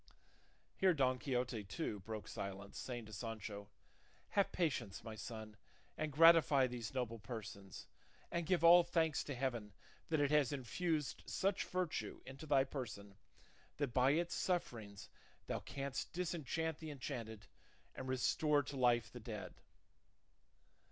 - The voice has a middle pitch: No, low, 130 Hz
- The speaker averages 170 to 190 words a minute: No, average, 140 wpm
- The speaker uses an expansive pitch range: Yes, wide, 5.9 semitones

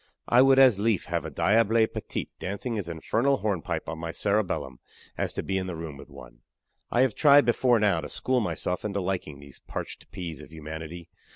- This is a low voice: Yes, very low, 95 Hz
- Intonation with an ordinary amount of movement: No, wide, 5.8 semitones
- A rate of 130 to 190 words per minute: No, average, 200 wpm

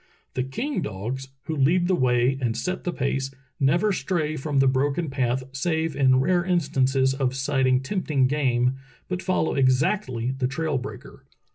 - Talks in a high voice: No, low, 135 Hz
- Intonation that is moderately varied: Yes, average, 3.6 semitones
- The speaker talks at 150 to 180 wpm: Yes, average, 160 wpm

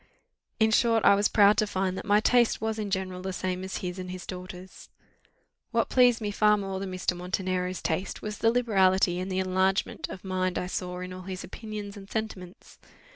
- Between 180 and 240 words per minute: Yes, fast, 205 wpm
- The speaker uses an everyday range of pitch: No, narrow, 2.3 semitones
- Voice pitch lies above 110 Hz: Yes, high, 190 Hz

